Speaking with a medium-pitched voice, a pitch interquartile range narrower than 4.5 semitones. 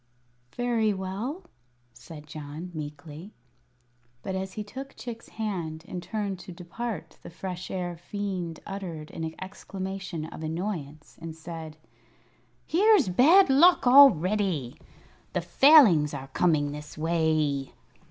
No: medium, 180 Hz; average, 5.1 semitones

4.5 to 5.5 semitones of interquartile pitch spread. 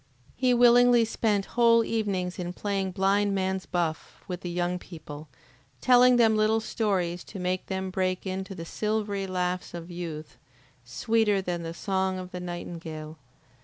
No: average, 3.3 semitones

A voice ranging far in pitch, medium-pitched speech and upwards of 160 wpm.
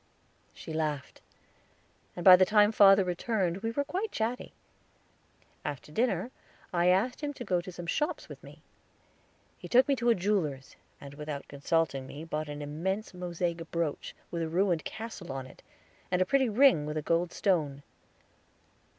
Yes: wide, 5.9 semitones; medium, 180 Hz; average, 170 wpm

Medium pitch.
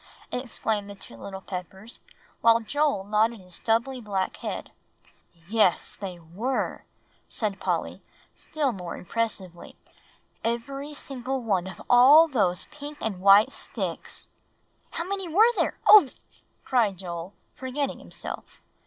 No: high, 225 Hz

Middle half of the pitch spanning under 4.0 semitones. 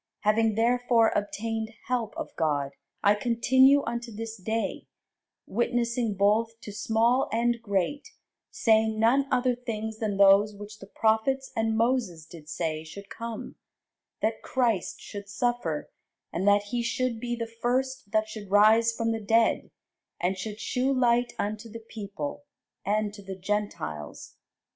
Yes: narrow, 2.6 semitones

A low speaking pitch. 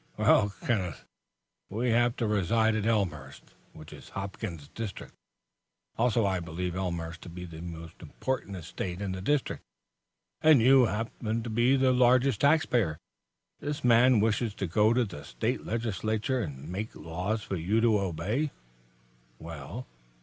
Yes: low, 105 Hz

